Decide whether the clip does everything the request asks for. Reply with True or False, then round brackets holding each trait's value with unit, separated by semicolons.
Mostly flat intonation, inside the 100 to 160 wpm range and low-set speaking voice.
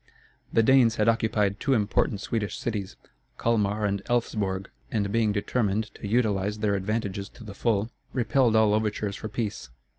True (2.1 semitones; 155 wpm; 105 Hz)